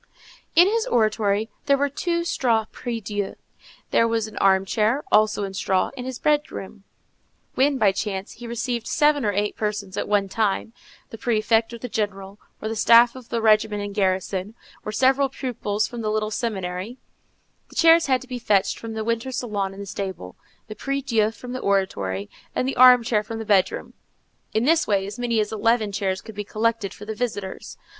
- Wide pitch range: No, average, 3.3 semitones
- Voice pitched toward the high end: Yes, high, 220 Hz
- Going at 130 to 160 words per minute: No, average, 195 wpm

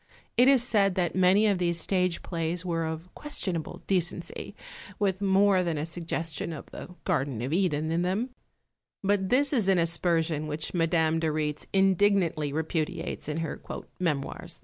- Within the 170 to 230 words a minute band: No, average, 160 wpm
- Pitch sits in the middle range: Yes, medium, 175 Hz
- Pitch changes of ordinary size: Yes, average, 3.2 semitones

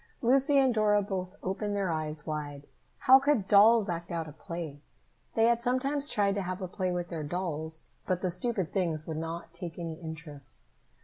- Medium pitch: Yes, medium, 180 Hz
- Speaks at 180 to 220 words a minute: Yes, average, 185 wpm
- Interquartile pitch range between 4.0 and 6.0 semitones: Yes, average, 4.7 semitones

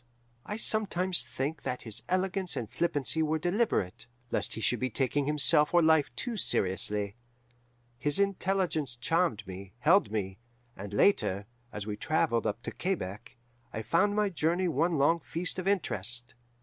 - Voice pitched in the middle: Yes, medium, 150 Hz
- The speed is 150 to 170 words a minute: Yes, average, 155 wpm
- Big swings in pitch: Yes, wide, 8.4 semitones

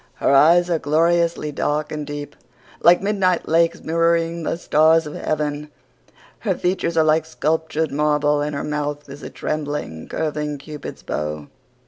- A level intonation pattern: Yes, narrow, 2.1 semitones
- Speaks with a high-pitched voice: No, medium, 155 Hz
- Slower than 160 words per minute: Yes, average, 150 wpm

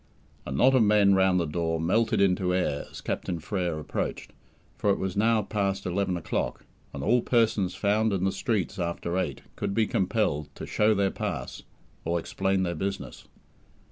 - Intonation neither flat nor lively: Yes, average, 3.4 semitones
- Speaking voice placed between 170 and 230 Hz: No, very low, 95 Hz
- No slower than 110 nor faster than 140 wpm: No, average, 175 wpm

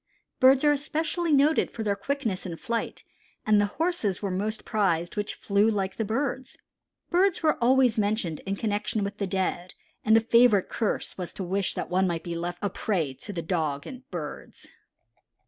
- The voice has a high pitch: Yes, high, 205 Hz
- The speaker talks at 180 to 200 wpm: Yes, average, 185 wpm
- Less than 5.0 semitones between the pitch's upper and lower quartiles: No, average, 5.3 semitones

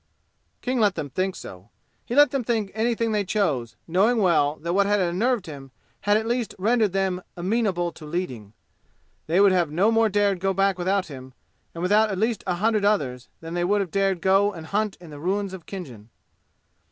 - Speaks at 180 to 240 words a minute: Yes, average, 200 wpm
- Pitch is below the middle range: No, high, 195 Hz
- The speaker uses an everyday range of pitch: Yes, average, 3.8 semitones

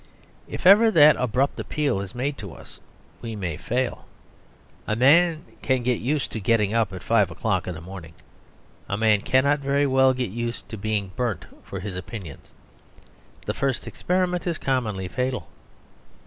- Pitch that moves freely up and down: Yes, wide, 5.7 semitones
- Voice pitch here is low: Yes, low, 120 Hz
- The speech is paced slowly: No, average, 165 wpm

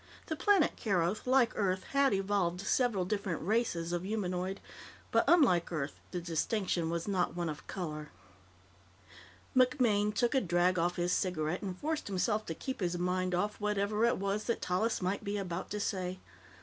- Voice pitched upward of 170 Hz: Yes, high, 190 Hz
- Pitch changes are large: No, average, 3.3 semitones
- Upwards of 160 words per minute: Yes, average, 170 wpm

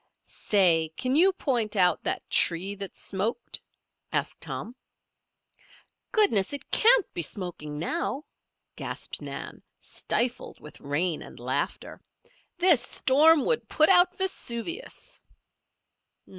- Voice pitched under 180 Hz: No, high, 235 Hz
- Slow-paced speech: Yes, slow, 110 wpm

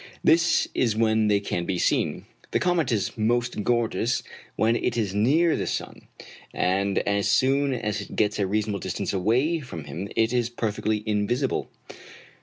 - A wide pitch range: No, average, 3.2 semitones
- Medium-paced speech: Yes, average, 165 wpm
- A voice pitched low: Yes, low, 110 Hz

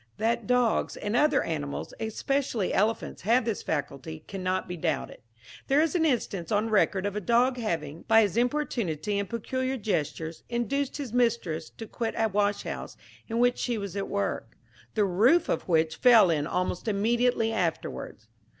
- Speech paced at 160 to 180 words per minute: Yes, average, 165 wpm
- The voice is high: Yes, high, 215 Hz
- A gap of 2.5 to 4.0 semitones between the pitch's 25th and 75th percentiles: No, average, 5.1 semitones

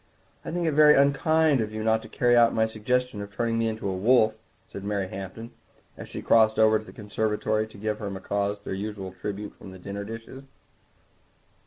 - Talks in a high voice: No, low, 110 Hz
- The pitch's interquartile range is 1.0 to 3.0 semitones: Yes, narrow, 2.5 semitones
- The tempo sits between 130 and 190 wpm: No, fast, 205 wpm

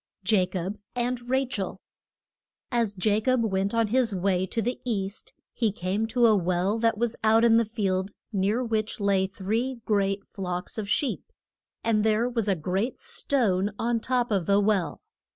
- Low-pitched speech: No, high, 215 Hz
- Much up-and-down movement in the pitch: No, average, 3.2 semitones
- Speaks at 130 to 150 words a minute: No, average, 170 wpm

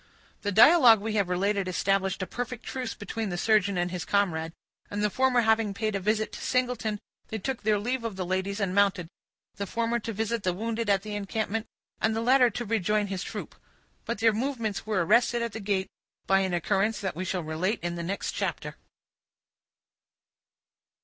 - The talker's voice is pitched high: Yes, high, 210 Hz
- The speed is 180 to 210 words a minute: Yes, average, 195 wpm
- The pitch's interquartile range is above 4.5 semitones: No, average, 2.9 semitones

